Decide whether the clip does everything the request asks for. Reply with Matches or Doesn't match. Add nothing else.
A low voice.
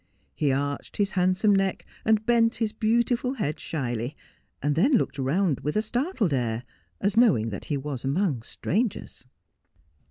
Doesn't match